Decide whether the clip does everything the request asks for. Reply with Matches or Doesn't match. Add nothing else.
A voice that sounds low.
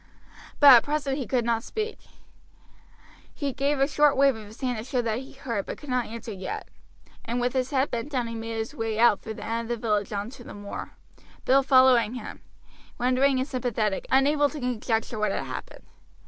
Doesn't match